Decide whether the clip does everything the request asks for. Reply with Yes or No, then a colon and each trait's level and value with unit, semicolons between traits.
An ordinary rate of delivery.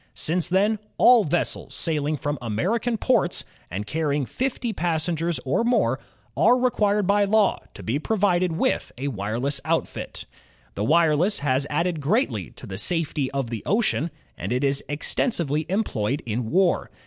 Yes: average, 150 wpm